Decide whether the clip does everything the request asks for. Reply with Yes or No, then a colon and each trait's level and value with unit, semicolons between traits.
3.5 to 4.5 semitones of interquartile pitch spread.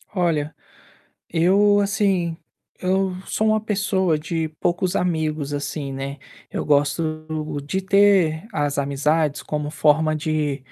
Yes: average, 4.2 semitones